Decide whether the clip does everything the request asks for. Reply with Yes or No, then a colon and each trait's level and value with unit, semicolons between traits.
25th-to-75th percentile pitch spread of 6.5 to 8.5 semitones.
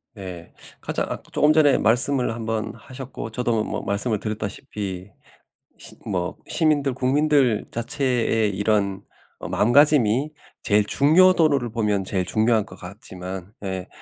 No: average, 5.2 semitones